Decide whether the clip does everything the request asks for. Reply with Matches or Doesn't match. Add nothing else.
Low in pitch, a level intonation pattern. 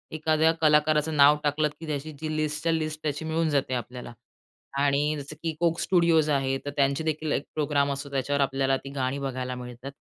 Doesn't match